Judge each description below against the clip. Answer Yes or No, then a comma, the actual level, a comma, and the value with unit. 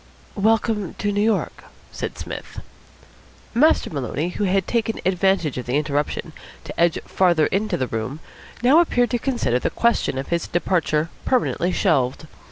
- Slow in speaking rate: No, average, 155 wpm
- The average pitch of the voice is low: No, medium, 180 Hz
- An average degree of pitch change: No, wide, 6.6 semitones